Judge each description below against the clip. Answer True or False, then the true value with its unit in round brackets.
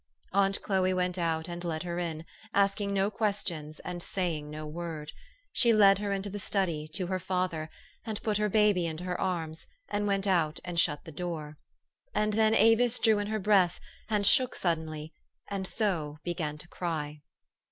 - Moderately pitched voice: True (180 Hz)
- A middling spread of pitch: True (3.9 semitones)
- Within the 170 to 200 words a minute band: True (180 wpm)